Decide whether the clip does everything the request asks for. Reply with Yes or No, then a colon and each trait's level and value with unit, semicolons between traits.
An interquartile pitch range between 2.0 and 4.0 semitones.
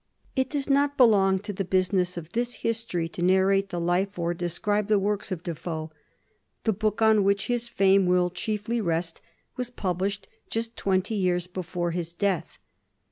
Yes: average, 3.4 semitones